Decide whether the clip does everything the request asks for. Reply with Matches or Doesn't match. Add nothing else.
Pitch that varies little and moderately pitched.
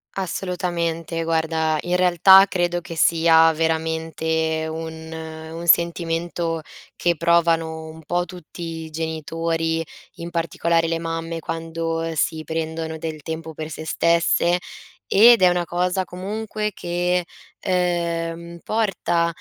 Matches